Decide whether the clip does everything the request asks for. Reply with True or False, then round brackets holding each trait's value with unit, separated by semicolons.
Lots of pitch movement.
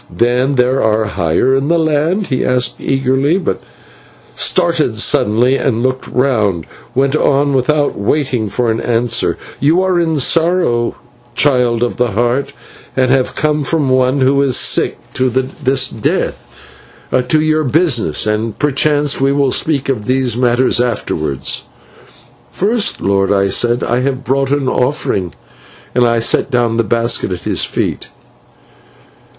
False (3.4 semitones)